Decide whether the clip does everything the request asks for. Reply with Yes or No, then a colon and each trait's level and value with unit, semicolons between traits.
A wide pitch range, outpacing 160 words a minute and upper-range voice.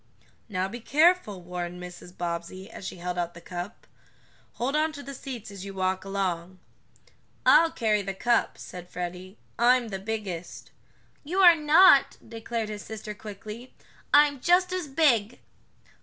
No: wide, 6.6 semitones; average, 155 wpm; high, 210 Hz